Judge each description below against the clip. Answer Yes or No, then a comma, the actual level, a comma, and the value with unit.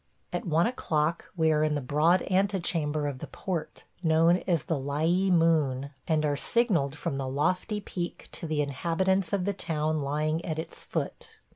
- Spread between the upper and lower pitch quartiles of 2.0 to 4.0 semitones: Yes, average, 3.3 semitones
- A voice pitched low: No, medium, 160 Hz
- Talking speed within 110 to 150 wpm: No, average, 175 wpm